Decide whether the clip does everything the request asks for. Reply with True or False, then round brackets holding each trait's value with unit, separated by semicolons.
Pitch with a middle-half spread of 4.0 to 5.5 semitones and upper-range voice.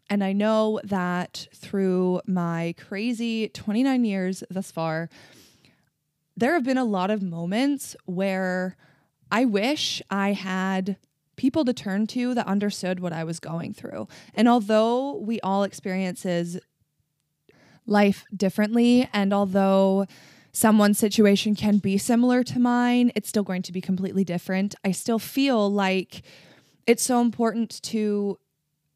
False (3.4 semitones; 195 Hz)